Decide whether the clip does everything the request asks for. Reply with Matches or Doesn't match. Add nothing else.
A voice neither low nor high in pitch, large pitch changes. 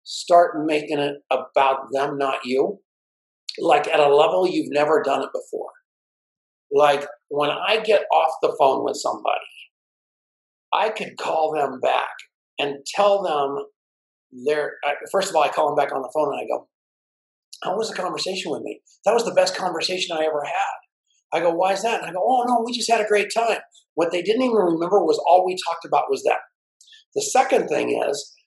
Matches